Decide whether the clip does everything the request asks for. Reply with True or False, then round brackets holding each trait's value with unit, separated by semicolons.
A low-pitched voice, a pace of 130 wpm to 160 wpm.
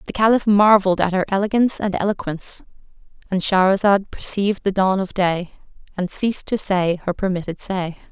False (195 Hz; 155 wpm)